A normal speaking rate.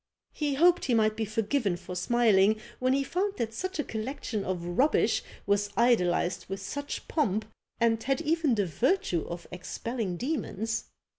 Yes: average, 160 wpm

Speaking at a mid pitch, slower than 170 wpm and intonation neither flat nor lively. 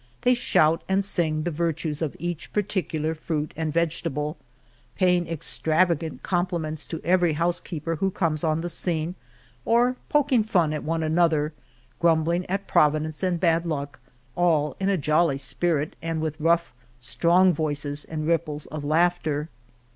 No: medium, 165 Hz; average, 155 wpm; narrow, 2.3 semitones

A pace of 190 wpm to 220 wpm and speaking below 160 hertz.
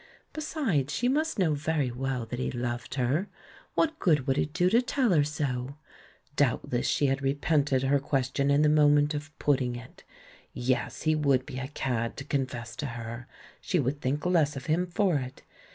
Yes: average, 200 wpm; medium, 140 Hz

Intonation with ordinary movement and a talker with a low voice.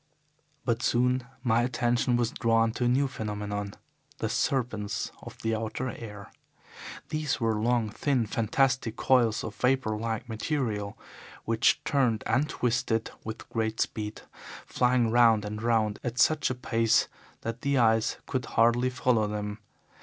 No: narrow, 2.3 semitones; low, 115 Hz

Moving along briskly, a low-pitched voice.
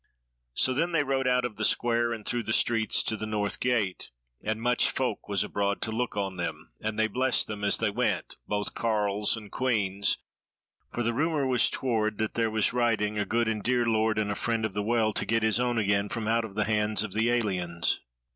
Yes: fast, 225 wpm; low, 110 Hz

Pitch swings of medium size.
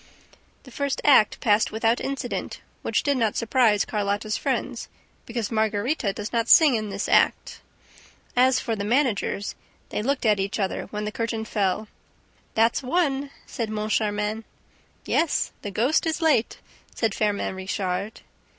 Yes: average, 3.5 semitones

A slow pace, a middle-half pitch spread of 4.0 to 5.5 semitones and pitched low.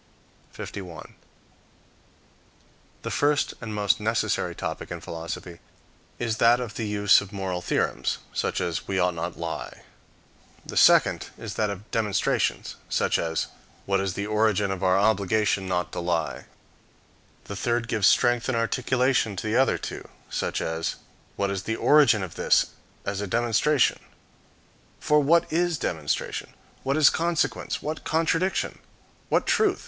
No: average, 150 wpm; average, 4.5 semitones; low, 105 Hz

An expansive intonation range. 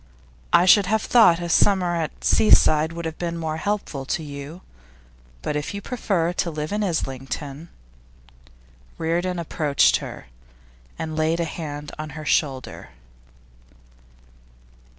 No: average, 3.1 semitones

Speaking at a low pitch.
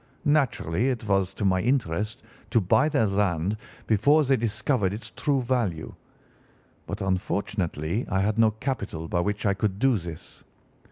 Yes: low, 105 Hz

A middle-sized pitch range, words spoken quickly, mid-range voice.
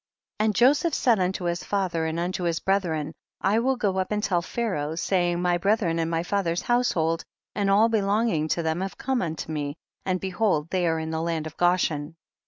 Yes: average, 3.7 semitones; fast, 215 wpm; medium, 180 Hz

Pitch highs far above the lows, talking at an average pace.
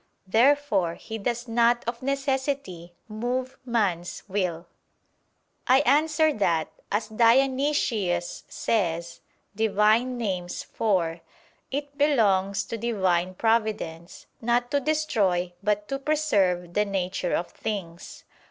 No: wide, 5.9 semitones; slow, 105 wpm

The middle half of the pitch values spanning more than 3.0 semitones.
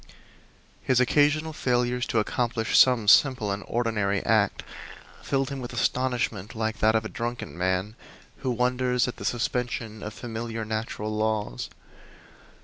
No: narrow, 2.6 semitones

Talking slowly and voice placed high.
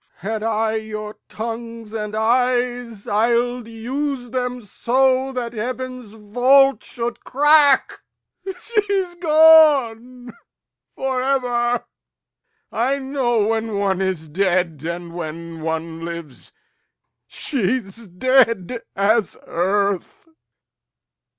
Yes: slow, 95 wpm; high, 230 Hz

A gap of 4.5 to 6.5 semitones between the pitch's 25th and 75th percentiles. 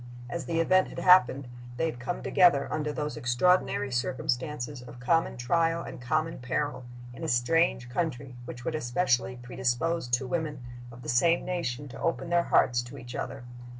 Yes: average, 5.1 semitones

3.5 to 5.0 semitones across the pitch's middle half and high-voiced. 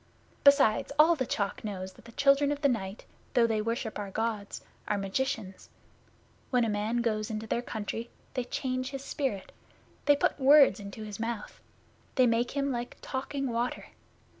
Yes: average, 4.0 semitones; high, 235 Hz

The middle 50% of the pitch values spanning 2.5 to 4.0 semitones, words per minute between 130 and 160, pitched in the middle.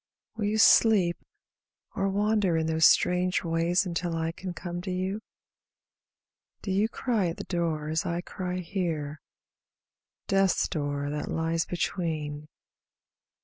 Yes: average, 2.9 semitones; slow, 135 wpm; medium, 175 Hz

